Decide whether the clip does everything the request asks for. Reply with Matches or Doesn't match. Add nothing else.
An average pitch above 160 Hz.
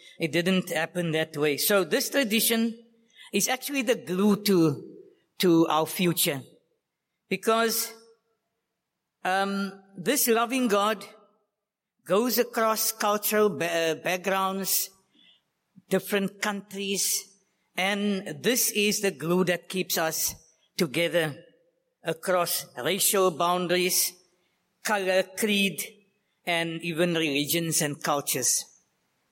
Matches